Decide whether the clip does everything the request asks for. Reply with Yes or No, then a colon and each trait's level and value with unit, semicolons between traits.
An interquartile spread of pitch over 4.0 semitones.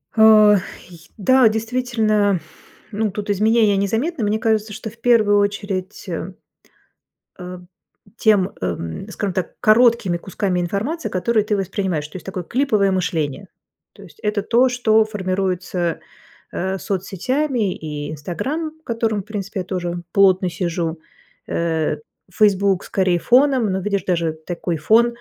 No: average, 3.5 semitones